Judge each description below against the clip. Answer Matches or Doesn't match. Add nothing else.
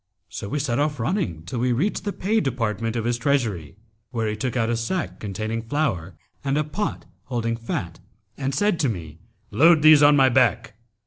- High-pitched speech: Doesn't match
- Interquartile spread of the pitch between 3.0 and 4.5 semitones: Doesn't match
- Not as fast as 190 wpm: Doesn't match